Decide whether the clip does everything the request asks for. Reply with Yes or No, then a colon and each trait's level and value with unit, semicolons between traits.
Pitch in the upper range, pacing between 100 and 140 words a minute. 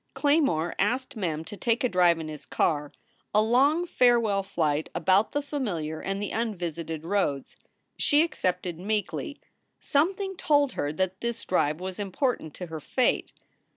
No: high, 195 Hz; average, 155 wpm